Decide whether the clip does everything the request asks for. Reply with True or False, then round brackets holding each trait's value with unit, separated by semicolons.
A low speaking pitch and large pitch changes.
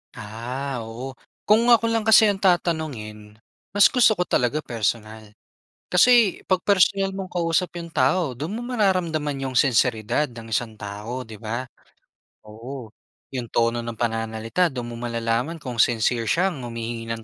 True (130 Hz; 7.8 semitones)